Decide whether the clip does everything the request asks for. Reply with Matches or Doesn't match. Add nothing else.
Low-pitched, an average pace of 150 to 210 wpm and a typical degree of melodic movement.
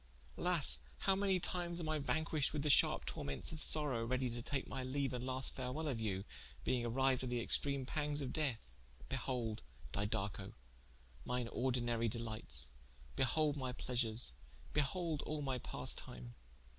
Matches